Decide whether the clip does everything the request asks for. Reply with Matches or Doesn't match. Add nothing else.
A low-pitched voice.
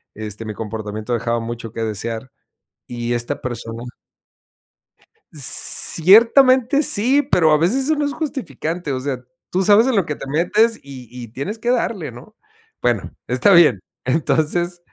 Doesn't match